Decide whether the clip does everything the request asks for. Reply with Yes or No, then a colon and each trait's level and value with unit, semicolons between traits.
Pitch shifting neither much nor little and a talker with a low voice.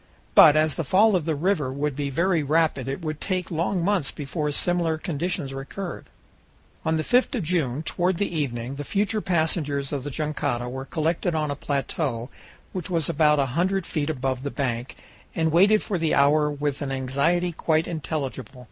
No: average, 3.8 semitones; medium, 155 Hz